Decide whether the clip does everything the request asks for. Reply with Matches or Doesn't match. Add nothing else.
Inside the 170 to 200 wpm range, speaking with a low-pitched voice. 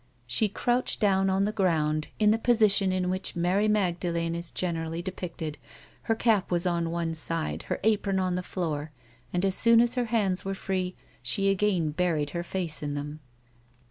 Doesn't match